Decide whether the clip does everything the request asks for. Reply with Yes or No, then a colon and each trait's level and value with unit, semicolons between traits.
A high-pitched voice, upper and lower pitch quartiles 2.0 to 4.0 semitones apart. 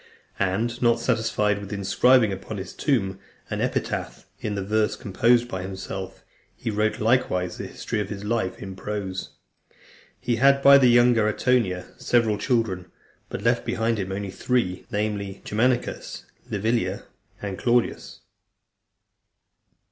No: low, 105 Hz; average, 3.6 semitones